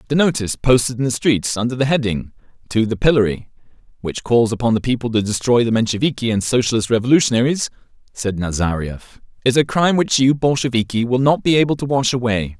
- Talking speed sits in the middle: Yes, average, 185 wpm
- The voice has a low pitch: Yes, low, 120 Hz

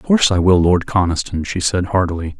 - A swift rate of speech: Yes, fast, 225 wpm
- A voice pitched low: Yes, very low, 95 Hz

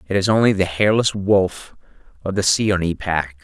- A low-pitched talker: Yes, very low, 95 Hz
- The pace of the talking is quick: No, average, 175 wpm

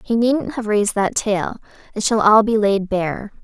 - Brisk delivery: Yes, fast, 210 wpm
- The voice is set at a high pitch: Yes, high, 215 Hz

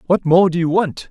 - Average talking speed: No, fast, 270 wpm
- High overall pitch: No, medium, 175 Hz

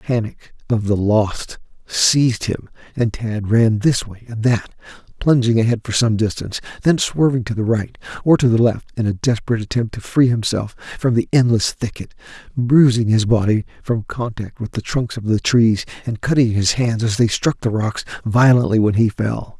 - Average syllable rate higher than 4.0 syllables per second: Yes, 5.1 syllables/s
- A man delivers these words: Yes, male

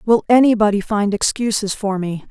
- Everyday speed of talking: Yes, average, 155 wpm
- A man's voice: No, female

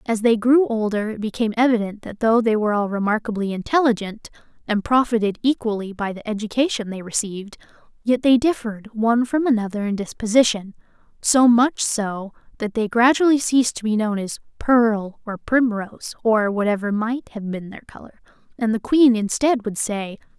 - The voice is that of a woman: Yes, female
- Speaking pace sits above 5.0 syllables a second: Yes, 5.3 syllables/s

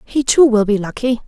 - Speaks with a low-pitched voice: No, high, 230 Hz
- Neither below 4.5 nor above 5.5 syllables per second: Yes, 5.3 syllables/s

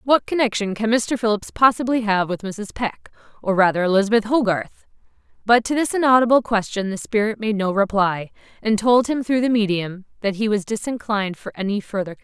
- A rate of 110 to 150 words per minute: No, average, 185 wpm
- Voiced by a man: No, female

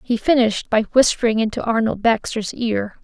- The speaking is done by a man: No, female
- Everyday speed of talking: Yes, average, 160 wpm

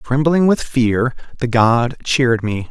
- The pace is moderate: Yes, average, 155 wpm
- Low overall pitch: Yes, low, 125 Hz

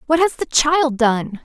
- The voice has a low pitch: No, very high, 270 Hz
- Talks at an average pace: No, fast, 210 wpm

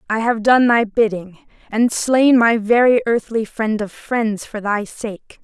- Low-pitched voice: No, high, 225 Hz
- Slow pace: No, average, 175 wpm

